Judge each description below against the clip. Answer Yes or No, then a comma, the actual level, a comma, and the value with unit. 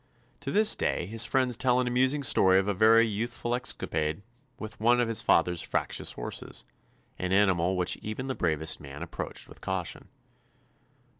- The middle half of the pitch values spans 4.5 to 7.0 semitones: Yes, average, 5.3 semitones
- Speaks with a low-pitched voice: Yes, low, 110 Hz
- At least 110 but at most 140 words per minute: No, average, 170 wpm